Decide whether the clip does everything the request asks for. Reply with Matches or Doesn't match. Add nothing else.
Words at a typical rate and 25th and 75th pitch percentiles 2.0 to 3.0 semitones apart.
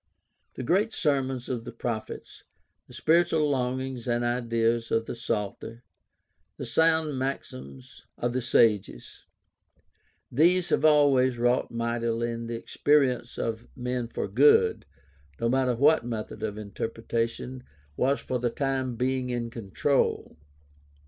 Doesn't match